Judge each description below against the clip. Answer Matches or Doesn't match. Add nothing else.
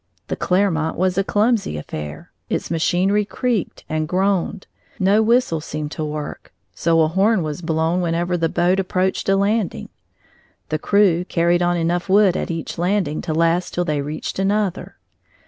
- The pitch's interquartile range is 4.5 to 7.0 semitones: Doesn't match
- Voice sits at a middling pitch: Matches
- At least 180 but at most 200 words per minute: Doesn't match